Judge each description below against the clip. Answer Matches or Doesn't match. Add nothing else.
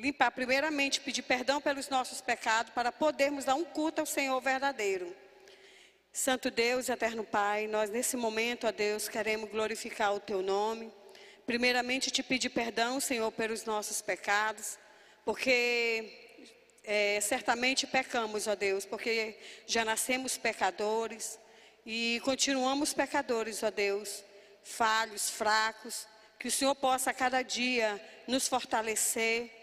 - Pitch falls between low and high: Doesn't match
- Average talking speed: Matches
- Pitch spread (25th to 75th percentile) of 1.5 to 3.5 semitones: Matches